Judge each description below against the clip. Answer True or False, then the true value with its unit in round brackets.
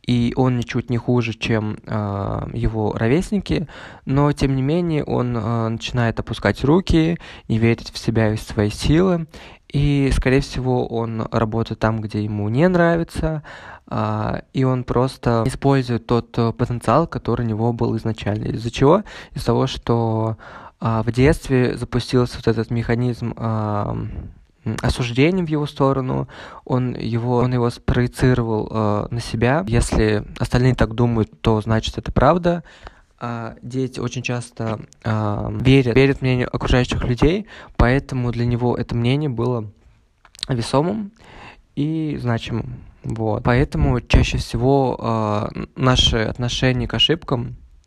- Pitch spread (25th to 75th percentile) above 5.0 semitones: False (2.9 semitones)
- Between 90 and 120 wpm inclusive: False (135 wpm)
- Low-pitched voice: True (120 Hz)